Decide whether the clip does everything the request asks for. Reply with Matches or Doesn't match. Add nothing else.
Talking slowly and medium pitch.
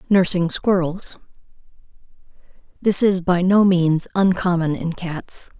Matches